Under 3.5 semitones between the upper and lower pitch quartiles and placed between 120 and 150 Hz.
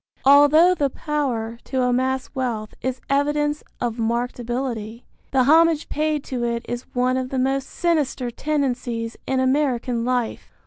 No: average, 3.1 semitones; very high, 260 Hz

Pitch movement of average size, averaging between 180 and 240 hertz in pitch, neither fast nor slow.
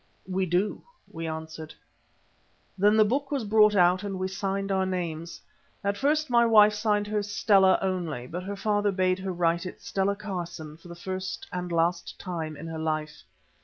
Yes: average, 3.4 semitones; medium, 185 Hz; average, 180 wpm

